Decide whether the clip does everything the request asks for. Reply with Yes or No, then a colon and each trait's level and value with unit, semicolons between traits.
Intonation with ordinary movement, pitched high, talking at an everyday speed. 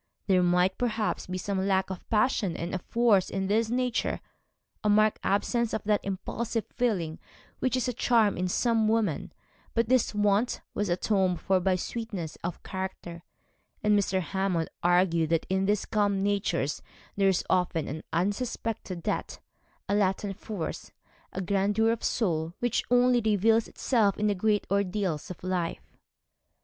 Yes: average, 3.3 semitones; high, 200 Hz; average, 160 wpm